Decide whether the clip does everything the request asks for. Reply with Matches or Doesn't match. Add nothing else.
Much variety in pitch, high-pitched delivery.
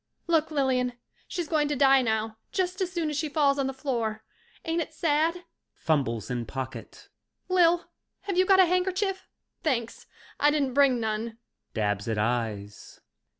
Matches